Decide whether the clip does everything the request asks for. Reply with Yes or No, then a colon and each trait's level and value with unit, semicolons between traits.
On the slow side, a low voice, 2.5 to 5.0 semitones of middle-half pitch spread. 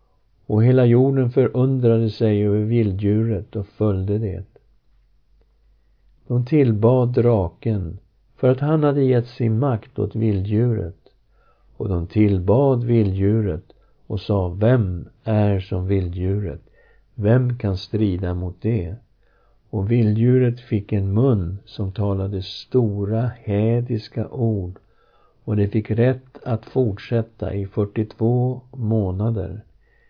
Yes: slow, 110 wpm; low, 110 Hz; average, 3.2 semitones